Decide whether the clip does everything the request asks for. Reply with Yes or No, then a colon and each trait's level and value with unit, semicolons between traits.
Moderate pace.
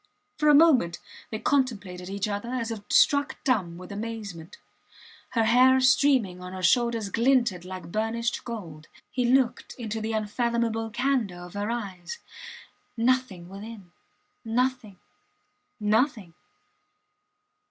No: slow, 120 wpm